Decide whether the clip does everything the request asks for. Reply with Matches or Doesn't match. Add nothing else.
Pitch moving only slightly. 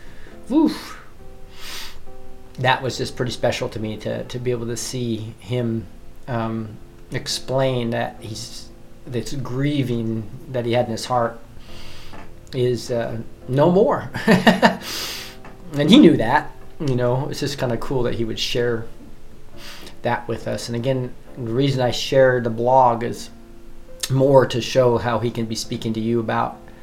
Matches